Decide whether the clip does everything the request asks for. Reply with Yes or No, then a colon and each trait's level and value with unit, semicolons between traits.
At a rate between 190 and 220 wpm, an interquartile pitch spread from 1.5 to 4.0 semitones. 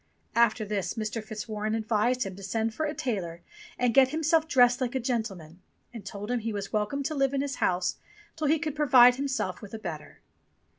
No: fast, 205 wpm; average, 4.4 semitones